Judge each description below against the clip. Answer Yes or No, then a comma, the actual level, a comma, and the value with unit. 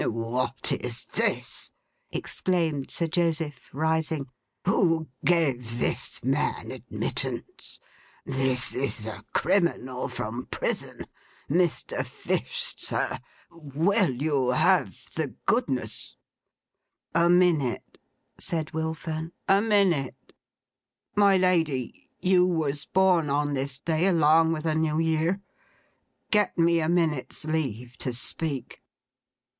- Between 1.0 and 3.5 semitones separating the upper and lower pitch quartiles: No, average, 4.1 semitones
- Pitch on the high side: No, medium, 160 Hz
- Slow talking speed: Yes, slow, 105 wpm